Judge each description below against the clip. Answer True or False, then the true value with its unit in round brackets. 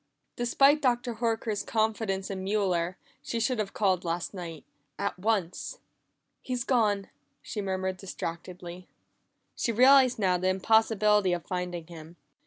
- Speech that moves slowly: True (130 wpm)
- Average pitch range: True (3.8 semitones)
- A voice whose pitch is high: True (195 Hz)